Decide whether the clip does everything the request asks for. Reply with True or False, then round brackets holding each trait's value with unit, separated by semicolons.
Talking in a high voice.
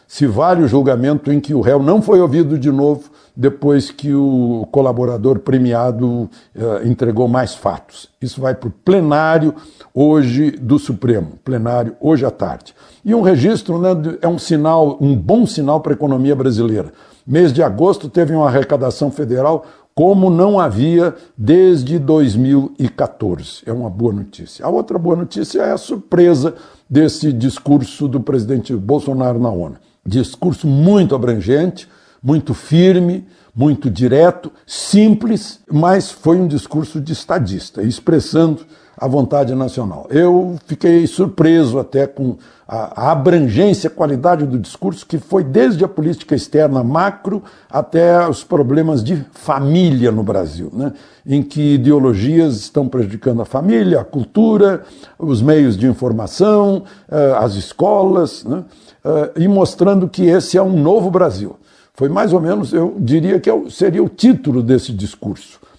False (150 Hz)